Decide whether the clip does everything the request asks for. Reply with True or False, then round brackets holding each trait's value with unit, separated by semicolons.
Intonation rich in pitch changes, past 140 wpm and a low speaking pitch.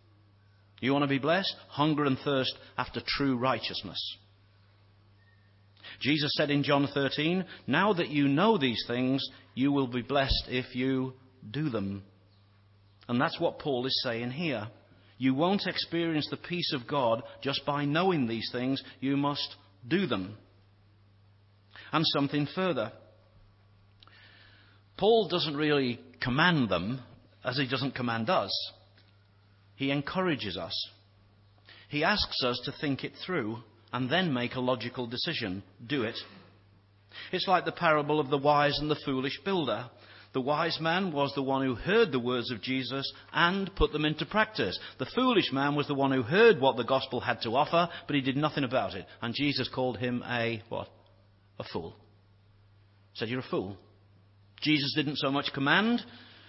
True (6.3 semitones; 160 wpm; 130 Hz)